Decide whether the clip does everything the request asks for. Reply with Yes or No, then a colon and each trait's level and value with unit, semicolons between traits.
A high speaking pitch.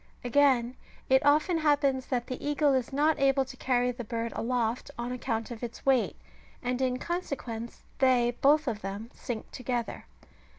Yes: very high, 255 Hz